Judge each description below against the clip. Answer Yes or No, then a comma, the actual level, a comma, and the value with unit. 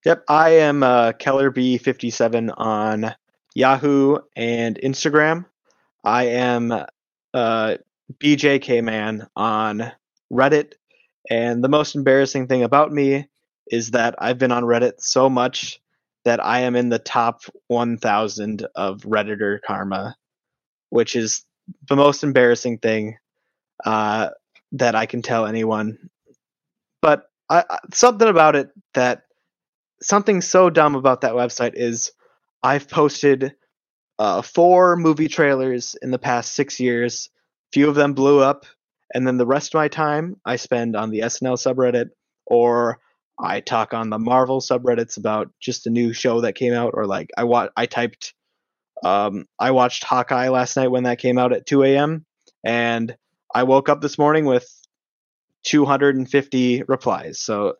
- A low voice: Yes, low, 125 Hz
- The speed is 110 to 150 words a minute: Yes, average, 145 wpm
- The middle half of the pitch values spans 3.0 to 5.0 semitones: Yes, average, 3.4 semitones